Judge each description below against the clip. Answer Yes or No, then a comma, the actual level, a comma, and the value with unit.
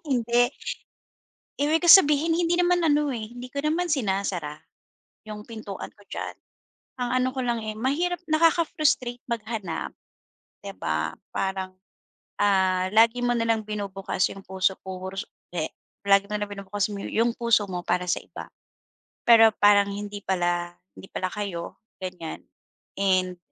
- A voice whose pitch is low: No, high, 210 Hz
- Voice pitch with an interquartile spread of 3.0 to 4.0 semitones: No, average, 4.6 semitones